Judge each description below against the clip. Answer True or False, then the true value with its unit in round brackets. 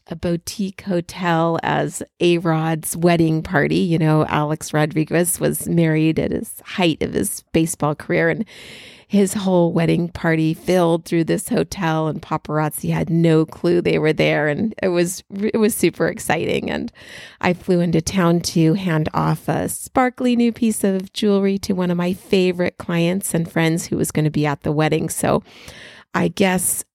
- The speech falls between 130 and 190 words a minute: True (175 wpm)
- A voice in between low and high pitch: True (170 Hz)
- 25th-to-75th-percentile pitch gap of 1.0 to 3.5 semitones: True (2.6 semitones)